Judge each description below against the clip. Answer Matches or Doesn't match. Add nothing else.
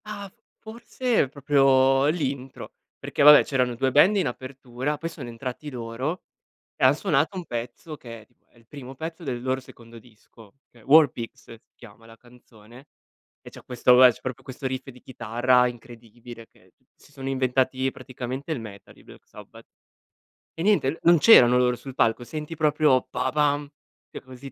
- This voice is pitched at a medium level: Doesn't match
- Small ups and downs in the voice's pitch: Doesn't match